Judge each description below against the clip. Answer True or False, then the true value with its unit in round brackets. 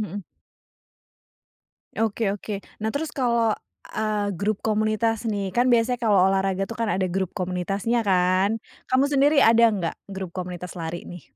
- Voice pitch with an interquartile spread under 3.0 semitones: False (3.3 semitones)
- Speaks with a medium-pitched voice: False (205 Hz)